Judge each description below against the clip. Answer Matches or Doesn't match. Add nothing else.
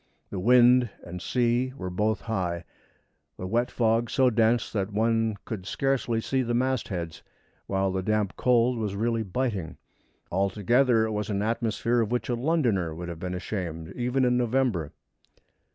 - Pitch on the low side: Matches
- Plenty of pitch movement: Doesn't match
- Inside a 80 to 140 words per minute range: Doesn't match